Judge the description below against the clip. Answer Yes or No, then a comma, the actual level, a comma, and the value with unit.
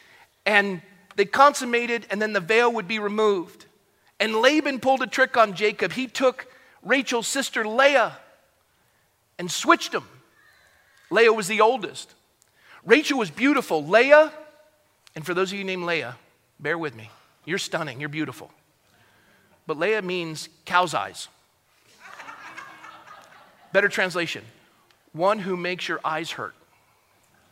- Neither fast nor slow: No, slow, 130 wpm